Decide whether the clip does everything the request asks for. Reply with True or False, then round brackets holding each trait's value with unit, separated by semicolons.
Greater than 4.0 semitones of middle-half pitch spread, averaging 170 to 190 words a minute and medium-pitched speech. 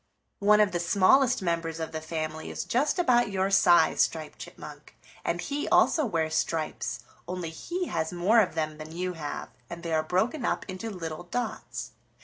True (4.9 semitones; 180 wpm; 175 Hz)